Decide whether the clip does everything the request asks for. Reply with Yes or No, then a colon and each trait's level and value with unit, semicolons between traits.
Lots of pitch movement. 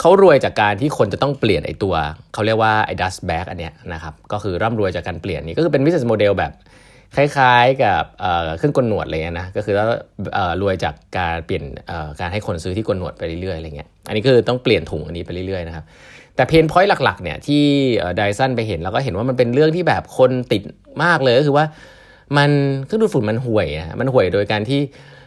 Yes: wide, 7.4 semitones